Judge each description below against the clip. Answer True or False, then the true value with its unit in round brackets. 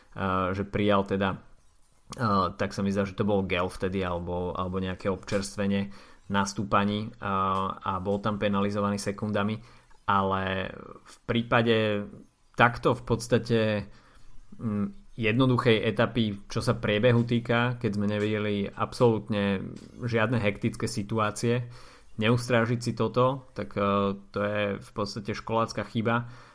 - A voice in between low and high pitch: False (105 Hz)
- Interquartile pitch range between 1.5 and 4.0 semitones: True (2.5 semitones)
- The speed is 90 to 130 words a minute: True (115 wpm)